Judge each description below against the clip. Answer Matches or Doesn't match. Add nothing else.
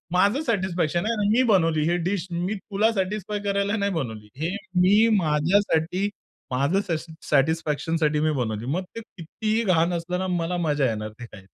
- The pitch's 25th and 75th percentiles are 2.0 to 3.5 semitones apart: Doesn't match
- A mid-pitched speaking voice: Matches